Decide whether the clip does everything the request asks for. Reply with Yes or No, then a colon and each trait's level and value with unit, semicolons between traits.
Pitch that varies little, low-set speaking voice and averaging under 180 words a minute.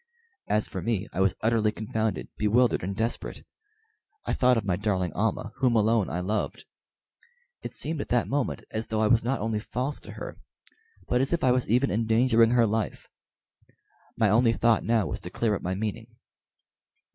No: narrow, 2.2 semitones; low, 110 Hz; average, 185 wpm